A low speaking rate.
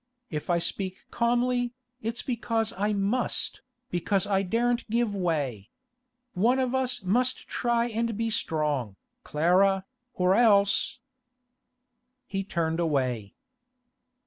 Yes: slow, 115 wpm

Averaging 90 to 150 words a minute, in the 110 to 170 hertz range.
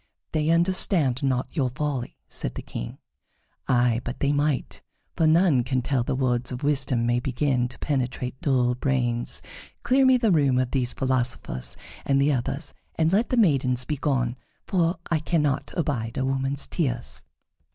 No: average, 160 wpm; low, 135 Hz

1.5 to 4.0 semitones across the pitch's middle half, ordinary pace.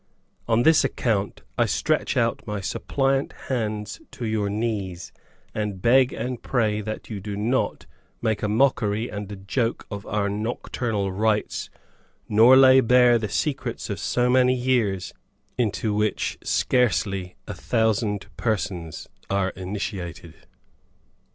No: average, 3.3 semitones; slow, 130 wpm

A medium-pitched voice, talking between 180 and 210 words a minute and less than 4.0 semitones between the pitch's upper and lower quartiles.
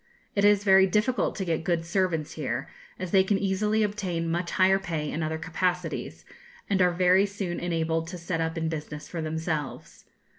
Yes: medium, 175 Hz; average, 185 wpm; average, 2.9 semitones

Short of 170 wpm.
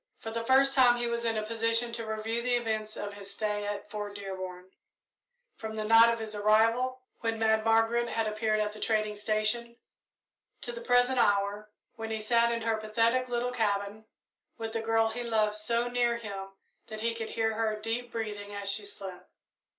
No: average, 195 wpm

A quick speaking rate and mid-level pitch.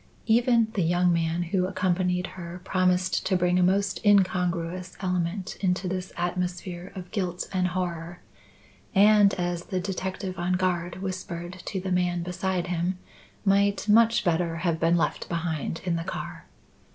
No: average, 150 wpm; medium, 180 Hz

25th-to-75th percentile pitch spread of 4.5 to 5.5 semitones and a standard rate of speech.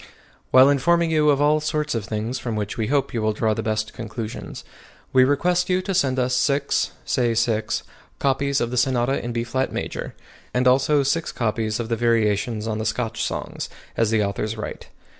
No: average, 4.1 semitones; average, 195 wpm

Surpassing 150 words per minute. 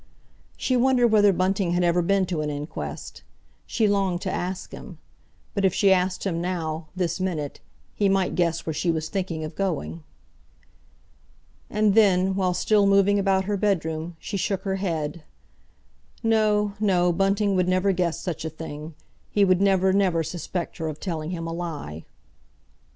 Yes: average, 165 wpm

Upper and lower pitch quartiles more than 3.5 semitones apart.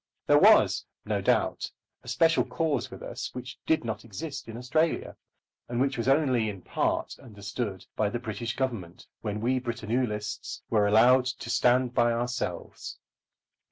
No: average, 2.9 semitones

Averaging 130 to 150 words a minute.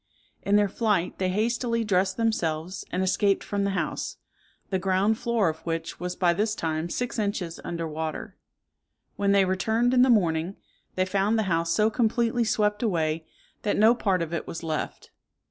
No: average, 180 wpm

